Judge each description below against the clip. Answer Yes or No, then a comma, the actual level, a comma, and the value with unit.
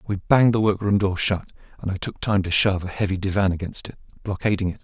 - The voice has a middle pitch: No, low, 100 Hz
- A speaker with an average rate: No, fast, 235 wpm